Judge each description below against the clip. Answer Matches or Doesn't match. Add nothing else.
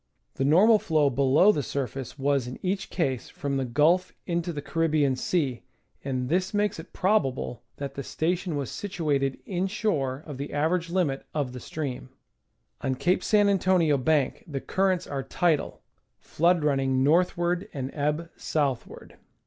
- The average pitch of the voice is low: Doesn't match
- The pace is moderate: Matches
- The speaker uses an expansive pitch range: Doesn't match